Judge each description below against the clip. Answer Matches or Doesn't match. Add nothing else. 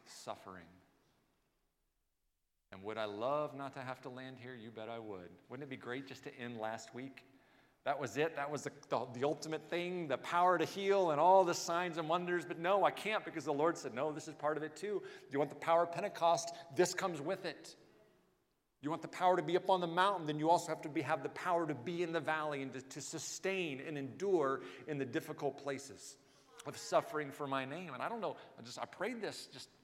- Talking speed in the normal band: Doesn't match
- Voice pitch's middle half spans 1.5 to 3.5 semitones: Doesn't match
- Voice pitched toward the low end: Doesn't match